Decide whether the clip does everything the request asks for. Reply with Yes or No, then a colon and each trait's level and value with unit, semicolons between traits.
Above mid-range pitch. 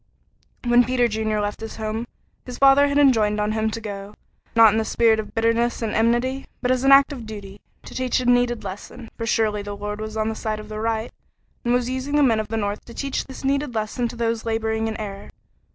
Yes: high, 225 Hz